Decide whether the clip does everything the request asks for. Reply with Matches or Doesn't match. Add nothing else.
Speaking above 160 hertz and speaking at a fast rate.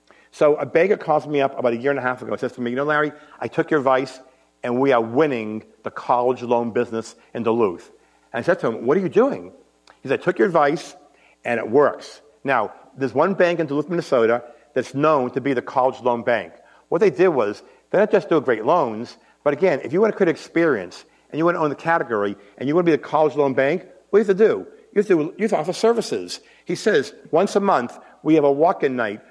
Doesn't match